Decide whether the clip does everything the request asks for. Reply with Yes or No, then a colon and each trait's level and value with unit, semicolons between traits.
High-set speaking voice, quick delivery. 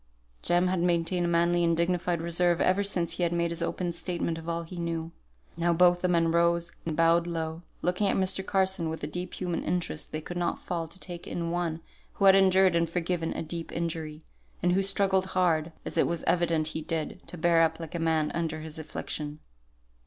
No: medium, 170 Hz; fast, 215 wpm